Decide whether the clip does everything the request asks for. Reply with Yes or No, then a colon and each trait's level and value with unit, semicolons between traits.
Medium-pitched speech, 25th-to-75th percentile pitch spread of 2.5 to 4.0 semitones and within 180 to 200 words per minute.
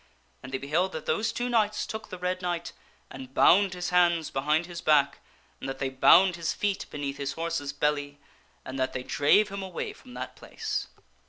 No: medium, 165 Hz; average, 4.9 semitones; average, 195 wpm